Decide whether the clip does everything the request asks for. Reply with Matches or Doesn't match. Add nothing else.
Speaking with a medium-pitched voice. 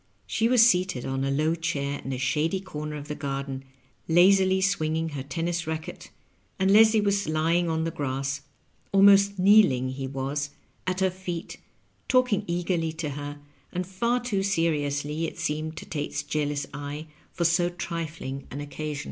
Matches